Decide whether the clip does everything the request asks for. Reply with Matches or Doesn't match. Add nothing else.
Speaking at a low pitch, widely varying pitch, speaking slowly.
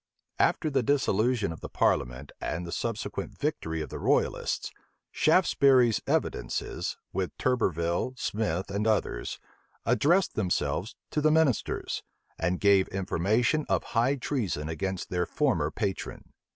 Matches